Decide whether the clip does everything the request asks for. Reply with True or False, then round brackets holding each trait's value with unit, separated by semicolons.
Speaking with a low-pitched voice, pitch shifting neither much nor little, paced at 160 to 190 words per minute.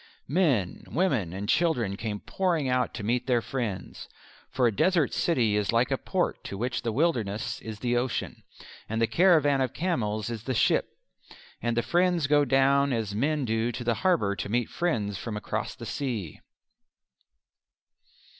True (120 Hz; 4.8 semitones; 170 wpm)